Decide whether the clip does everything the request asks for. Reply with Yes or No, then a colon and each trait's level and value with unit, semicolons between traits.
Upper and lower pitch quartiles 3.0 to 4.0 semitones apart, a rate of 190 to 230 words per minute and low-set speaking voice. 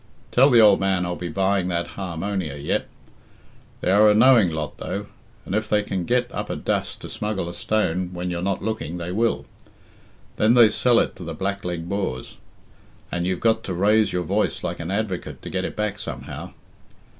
Yes: average, 3.5 semitones; average, 200 wpm; very low, 95 Hz